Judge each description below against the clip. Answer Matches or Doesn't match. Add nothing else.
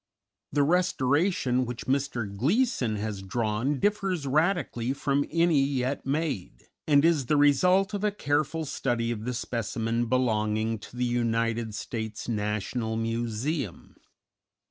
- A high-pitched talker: Doesn't match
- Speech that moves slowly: Matches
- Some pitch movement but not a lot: Matches